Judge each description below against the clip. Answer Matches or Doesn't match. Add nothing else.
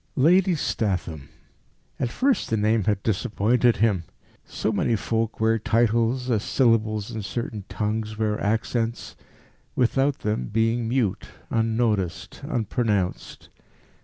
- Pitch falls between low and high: Doesn't match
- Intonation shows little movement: Matches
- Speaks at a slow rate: Matches